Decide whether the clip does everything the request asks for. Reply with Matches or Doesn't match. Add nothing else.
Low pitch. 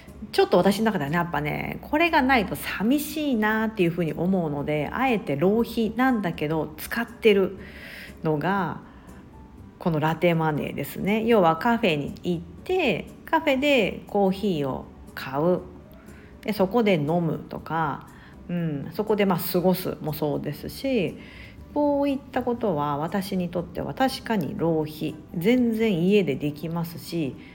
Doesn't match